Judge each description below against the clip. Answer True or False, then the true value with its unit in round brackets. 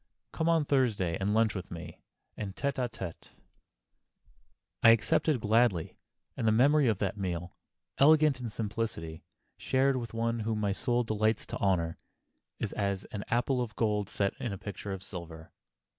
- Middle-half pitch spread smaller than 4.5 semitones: True (3.9 semitones)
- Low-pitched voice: True (110 Hz)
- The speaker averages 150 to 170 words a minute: True (165 wpm)